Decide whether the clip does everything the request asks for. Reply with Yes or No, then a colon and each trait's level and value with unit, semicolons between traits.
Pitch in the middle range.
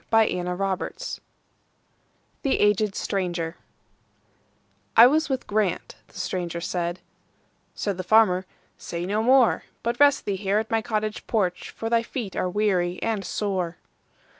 No: high, 200 Hz